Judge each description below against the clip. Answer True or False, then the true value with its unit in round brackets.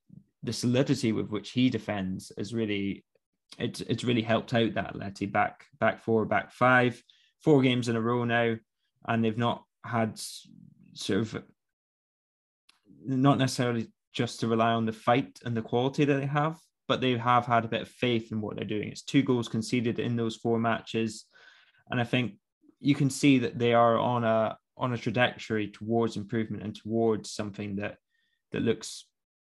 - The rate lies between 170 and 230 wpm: True (180 wpm)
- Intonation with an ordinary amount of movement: False (2.3 semitones)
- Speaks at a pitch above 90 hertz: True (115 Hz)